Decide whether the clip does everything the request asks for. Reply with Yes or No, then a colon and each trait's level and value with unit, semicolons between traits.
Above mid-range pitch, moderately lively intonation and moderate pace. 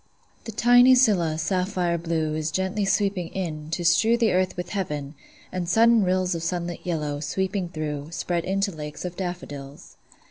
No: medium, 180 Hz; average, 3.4 semitones; average, 165 wpm